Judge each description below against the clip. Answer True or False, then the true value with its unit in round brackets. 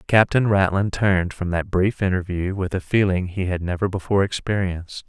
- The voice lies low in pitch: True (95 Hz)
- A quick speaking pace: False (175 wpm)